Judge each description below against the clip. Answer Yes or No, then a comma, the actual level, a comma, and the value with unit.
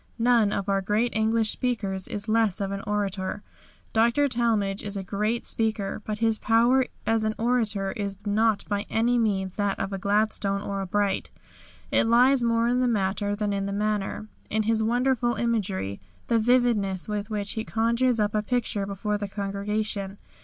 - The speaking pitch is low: No, high, 215 Hz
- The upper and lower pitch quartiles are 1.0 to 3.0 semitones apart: Yes, narrow, 2.4 semitones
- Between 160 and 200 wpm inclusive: Yes, average, 180 wpm